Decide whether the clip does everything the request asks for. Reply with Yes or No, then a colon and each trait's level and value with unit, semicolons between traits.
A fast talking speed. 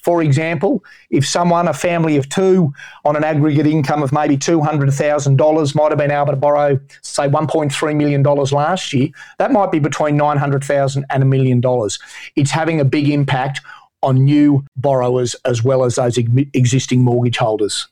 No: average, 165 wpm